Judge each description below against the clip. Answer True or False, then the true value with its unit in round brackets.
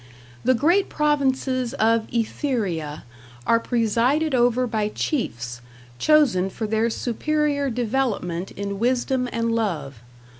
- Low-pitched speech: False (235 Hz)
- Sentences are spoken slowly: True (110 wpm)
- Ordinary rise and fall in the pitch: True (4.1 semitones)